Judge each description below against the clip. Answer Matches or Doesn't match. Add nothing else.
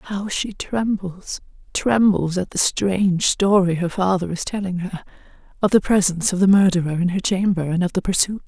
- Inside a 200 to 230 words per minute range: Doesn't match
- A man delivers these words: Doesn't match